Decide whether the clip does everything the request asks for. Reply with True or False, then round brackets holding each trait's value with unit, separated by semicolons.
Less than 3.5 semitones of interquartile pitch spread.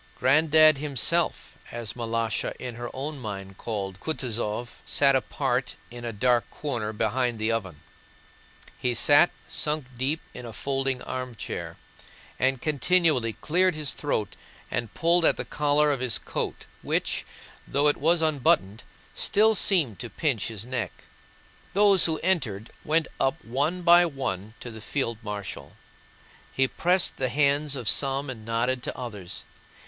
False (4.7 semitones)